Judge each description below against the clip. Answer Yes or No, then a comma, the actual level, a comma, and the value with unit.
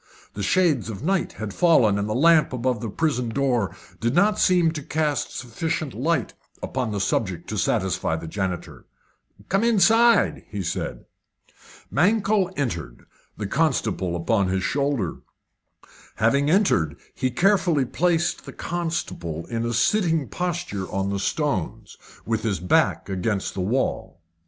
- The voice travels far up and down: Yes, wide, 8.7 semitones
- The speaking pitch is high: No, low, 125 Hz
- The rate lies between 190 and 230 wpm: No, average, 140 wpm